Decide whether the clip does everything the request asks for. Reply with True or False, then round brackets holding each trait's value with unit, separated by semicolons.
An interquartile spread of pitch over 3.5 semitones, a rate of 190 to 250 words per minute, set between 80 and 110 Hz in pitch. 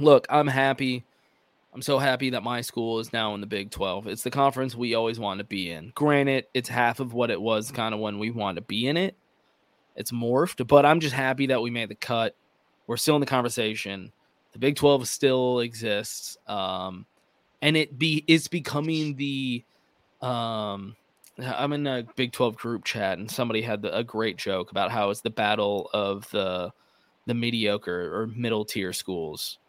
False (4.2 semitones; 195 wpm; 120 Hz)